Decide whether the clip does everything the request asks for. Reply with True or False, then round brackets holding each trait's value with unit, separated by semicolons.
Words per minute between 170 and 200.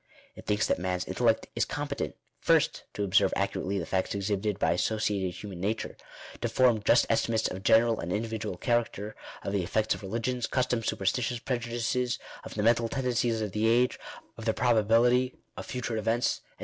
True (185 wpm)